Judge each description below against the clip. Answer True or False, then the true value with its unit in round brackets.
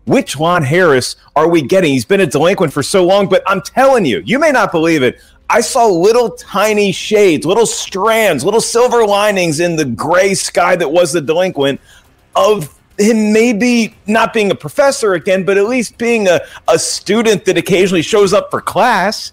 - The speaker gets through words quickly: False (190 wpm)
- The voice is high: True (195 Hz)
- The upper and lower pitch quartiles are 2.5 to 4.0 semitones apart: False (4.4 semitones)